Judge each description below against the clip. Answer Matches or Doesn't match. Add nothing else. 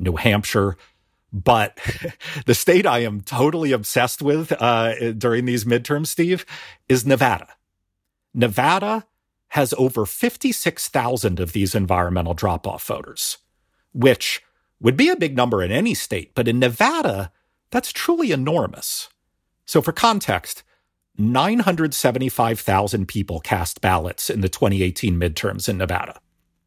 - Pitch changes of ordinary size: Doesn't match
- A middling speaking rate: Doesn't match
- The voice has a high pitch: Doesn't match